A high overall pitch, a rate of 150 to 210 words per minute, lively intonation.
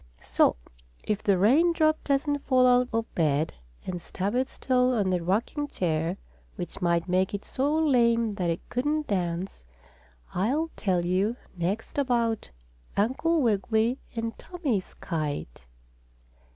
No: high, 220 Hz; average, 140 wpm; wide, 6.2 semitones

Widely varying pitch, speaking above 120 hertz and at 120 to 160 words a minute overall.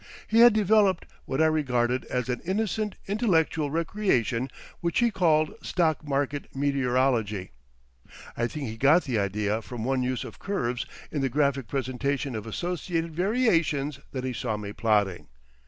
Yes: wide, 5.7 semitones; medium, 140 Hz; average, 155 wpm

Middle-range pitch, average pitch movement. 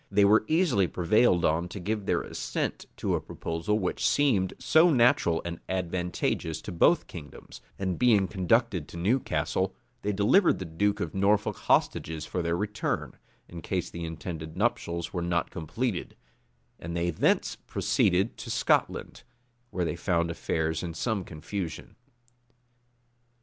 No: very low, 90 Hz; average, 3.9 semitones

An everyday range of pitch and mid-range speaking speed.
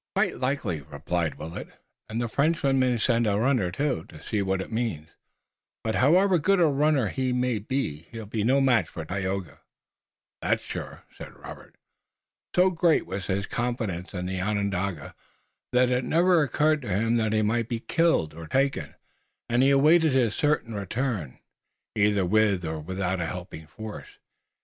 No: wide, 6.2 semitones; average, 170 wpm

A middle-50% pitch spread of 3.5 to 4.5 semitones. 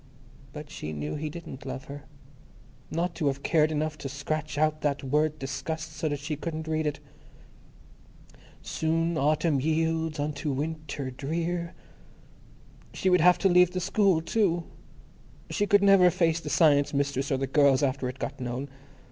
No: average, 2.7 semitones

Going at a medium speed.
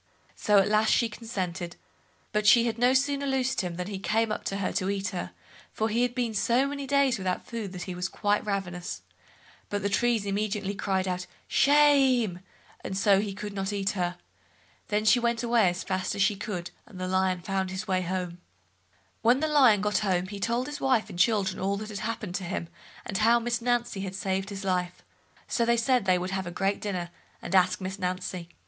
No: fast, 210 wpm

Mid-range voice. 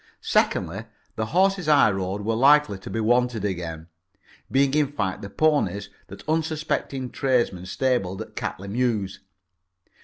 No: low, 115 Hz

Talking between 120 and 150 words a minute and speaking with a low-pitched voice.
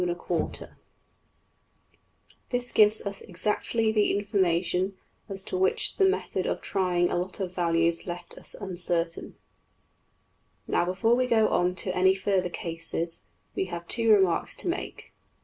No: average, 145 wpm; medium, 185 Hz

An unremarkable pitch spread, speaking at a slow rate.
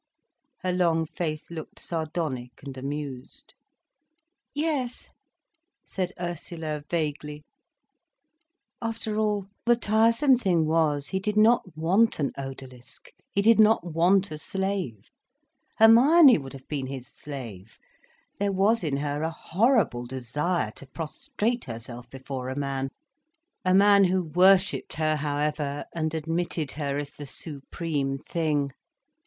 No: wide, 6.0 semitones; slow, 120 wpm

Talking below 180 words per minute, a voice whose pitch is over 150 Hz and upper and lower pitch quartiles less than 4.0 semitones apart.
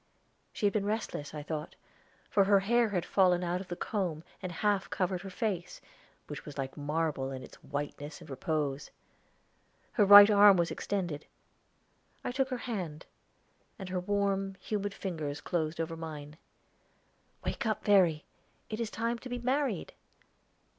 No: average, 160 wpm; medium, 185 Hz; average, 4.7 semitones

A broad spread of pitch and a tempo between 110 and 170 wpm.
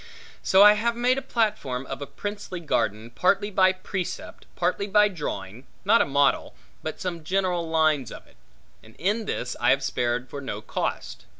No: wide, 7.3 semitones; average, 180 wpm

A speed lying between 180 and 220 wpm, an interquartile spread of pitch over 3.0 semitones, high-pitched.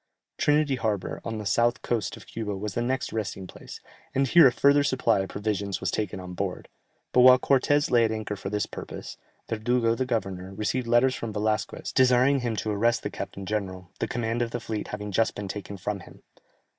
No: fast, 205 wpm; average, 3.4 semitones; low, 110 Hz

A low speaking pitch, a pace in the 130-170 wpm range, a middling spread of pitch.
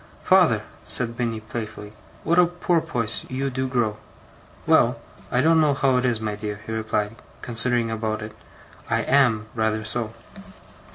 Yes: low, 115 Hz; average, 155 wpm; average, 3.3 semitones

